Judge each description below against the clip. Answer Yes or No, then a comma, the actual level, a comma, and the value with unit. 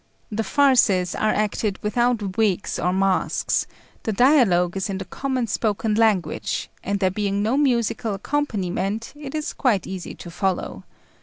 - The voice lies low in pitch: No, high, 210 Hz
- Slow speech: No, average, 150 wpm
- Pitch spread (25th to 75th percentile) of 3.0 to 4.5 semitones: Yes, average, 3.8 semitones